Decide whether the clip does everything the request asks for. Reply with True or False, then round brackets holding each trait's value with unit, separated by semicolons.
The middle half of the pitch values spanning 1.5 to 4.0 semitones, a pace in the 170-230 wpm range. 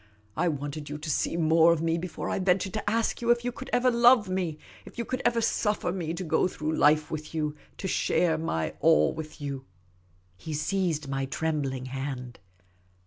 False (4.5 semitones; 200 wpm)